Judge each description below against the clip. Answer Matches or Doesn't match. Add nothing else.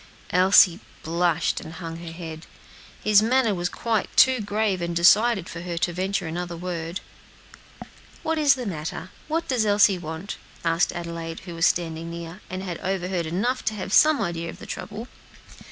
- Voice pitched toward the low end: Doesn't match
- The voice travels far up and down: Doesn't match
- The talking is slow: Doesn't match